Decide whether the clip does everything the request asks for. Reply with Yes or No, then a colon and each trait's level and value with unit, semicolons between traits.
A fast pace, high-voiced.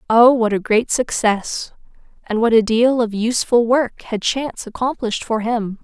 No: average, 175 wpm; high, 230 Hz